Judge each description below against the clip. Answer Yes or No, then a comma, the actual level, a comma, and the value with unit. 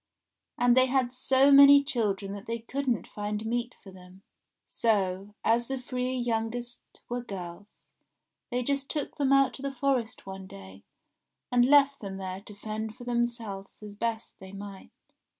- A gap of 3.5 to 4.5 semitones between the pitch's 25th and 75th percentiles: Yes, average, 4.1 semitones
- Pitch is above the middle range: Yes, high, 235 Hz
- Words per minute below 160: No, average, 165 wpm